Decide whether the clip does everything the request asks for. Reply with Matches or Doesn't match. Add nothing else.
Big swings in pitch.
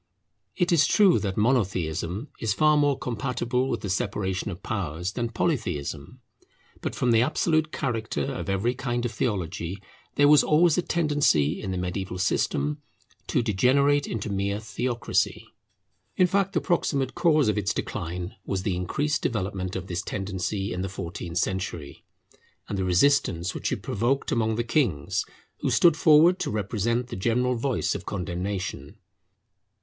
Matches